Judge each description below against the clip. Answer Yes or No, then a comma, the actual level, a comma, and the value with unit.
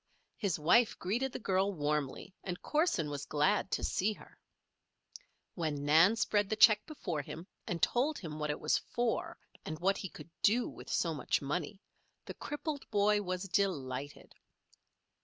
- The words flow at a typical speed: Yes, average, 160 wpm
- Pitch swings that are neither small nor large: No, wide, 5.7 semitones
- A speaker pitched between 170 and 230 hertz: Yes, medium, 185 Hz